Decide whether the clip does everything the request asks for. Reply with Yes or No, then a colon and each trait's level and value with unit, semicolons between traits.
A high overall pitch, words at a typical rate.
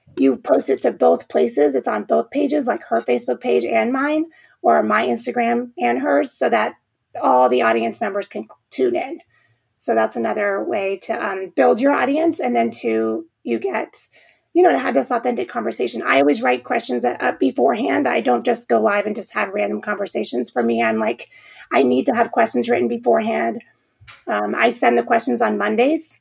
Yes: high, 200 Hz; average, 195 wpm